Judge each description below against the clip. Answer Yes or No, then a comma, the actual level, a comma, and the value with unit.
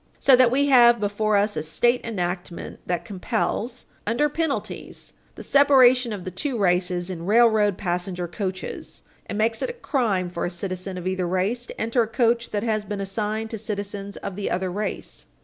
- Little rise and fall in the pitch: No, average, 4.2 semitones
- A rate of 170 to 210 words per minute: Yes, average, 185 wpm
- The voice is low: No, high, 210 Hz